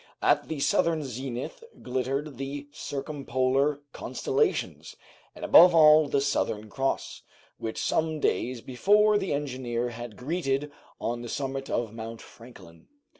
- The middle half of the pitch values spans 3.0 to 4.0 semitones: Yes, average, 3.6 semitones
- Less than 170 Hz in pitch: Yes, low, 135 Hz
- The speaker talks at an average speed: No, slow, 125 wpm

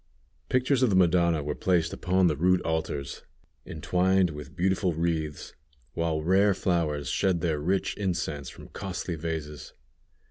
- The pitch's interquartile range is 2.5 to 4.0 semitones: Yes, average, 3.2 semitones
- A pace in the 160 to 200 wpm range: No, average, 140 wpm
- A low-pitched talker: Yes, very low, 85 Hz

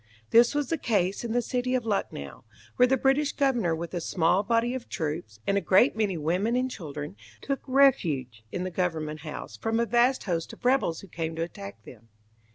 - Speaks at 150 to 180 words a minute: No, fast, 205 wpm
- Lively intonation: Yes, wide, 7.0 semitones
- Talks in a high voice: Yes, high, 200 Hz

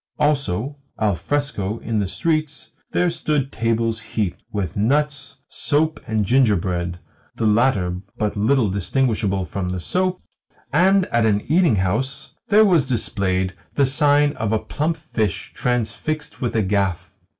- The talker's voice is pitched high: No, low, 115 Hz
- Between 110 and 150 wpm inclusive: Yes, average, 140 wpm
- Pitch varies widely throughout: Yes, wide, 6.4 semitones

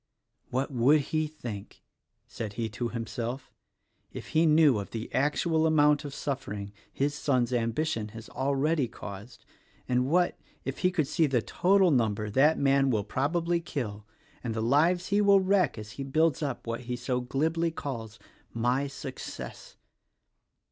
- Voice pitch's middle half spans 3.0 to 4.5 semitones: No, average, 5.1 semitones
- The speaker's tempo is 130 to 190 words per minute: Yes, average, 155 wpm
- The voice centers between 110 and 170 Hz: Yes, low, 135 Hz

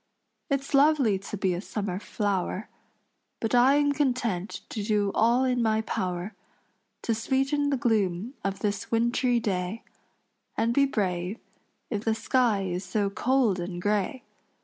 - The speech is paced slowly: No, average, 150 wpm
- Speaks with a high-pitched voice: Yes, high, 220 Hz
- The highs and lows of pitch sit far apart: No, average, 4.4 semitones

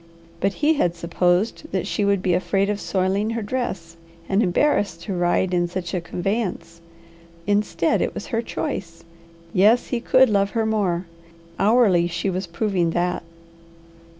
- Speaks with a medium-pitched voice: No, high, 195 Hz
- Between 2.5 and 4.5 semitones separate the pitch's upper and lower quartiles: Yes, average, 3.4 semitones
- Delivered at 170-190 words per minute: No, average, 155 wpm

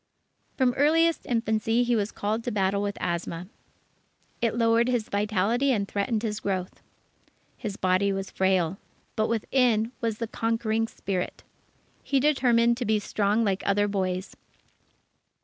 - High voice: Yes, high, 215 Hz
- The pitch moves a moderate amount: Yes, average, 3.0 semitones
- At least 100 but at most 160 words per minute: Yes, average, 140 wpm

